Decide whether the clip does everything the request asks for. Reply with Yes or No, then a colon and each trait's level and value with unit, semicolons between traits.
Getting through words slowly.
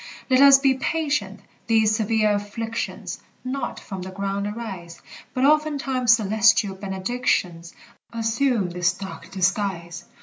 Yes: slow, 115 wpm